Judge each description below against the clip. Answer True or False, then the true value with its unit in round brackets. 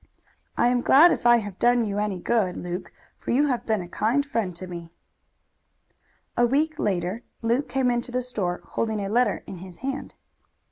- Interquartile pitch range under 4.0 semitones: False (4.8 semitones)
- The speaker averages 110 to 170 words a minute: False (190 wpm)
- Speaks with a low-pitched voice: False (230 Hz)